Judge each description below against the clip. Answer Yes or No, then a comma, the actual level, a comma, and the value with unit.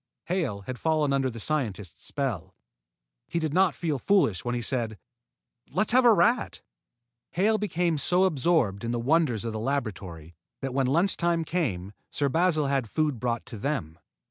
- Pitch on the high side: No, medium, 140 Hz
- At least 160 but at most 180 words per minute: Yes, average, 170 wpm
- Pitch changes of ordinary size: No, wide, 6.7 semitones